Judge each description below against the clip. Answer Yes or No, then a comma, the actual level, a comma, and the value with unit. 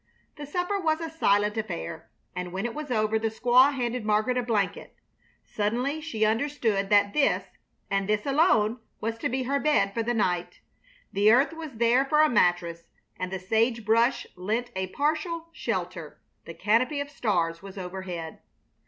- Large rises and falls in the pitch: Yes, wide, 5.7 semitones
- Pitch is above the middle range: Yes, high, 225 Hz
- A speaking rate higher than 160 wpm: Yes, average, 170 wpm